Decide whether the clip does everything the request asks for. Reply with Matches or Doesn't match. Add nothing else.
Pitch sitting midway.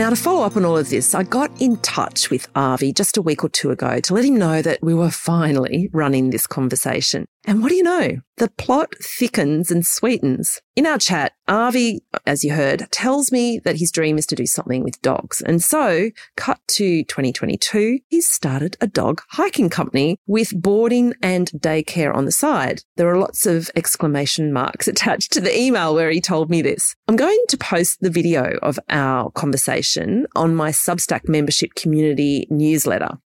Matches